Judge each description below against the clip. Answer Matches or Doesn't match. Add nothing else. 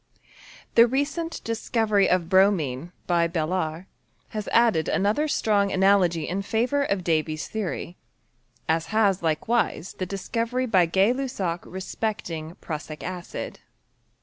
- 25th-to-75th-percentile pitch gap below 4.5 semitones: Doesn't match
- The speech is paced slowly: Matches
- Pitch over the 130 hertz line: Matches